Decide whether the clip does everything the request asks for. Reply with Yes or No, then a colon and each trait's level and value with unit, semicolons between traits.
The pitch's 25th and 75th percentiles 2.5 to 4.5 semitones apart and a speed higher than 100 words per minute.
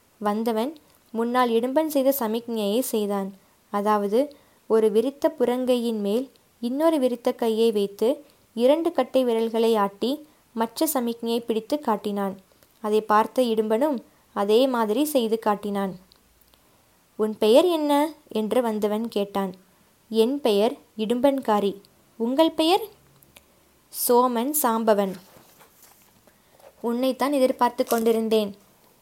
No: average, 3.2 semitones; average, 95 wpm